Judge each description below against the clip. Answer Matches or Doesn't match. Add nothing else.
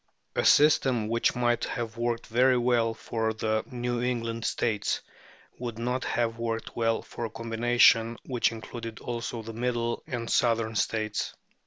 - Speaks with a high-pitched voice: Doesn't match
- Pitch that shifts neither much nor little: Doesn't match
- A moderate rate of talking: Matches